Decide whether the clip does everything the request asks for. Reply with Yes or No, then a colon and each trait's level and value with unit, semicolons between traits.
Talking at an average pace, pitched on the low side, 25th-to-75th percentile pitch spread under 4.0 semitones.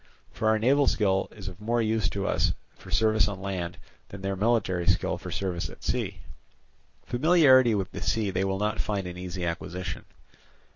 Yes: average, 185 wpm; low, 100 Hz; average, 3.2 semitones